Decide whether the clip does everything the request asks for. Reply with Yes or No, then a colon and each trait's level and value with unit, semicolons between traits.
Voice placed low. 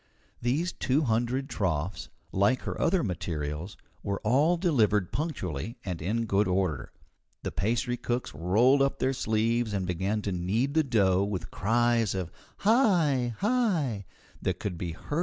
Yes: low, 110 Hz